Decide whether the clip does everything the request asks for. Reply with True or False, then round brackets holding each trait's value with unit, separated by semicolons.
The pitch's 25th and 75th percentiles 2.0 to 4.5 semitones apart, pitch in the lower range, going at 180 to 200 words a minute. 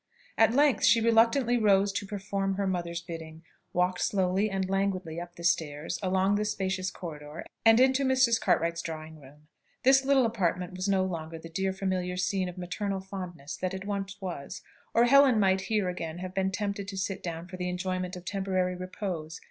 False (2.4 semitones; 190 Hz; 190 wpm)